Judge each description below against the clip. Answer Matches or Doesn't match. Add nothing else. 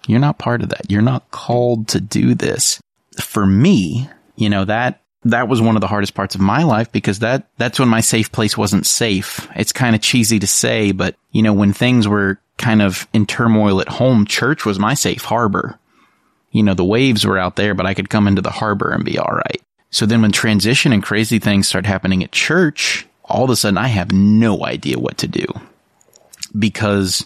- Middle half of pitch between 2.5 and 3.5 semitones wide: Matches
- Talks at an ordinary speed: Doesn't match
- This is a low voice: Matches